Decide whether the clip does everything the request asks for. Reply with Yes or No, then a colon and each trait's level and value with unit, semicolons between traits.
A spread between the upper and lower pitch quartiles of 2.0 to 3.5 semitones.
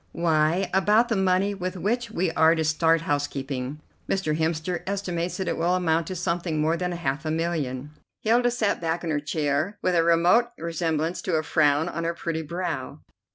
Yes: average, 2.8 semitones